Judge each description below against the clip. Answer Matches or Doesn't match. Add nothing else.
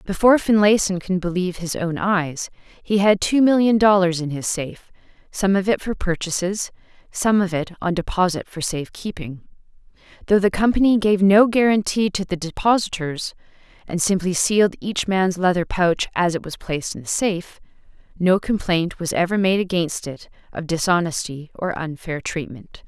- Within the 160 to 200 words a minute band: Matches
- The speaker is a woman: Matches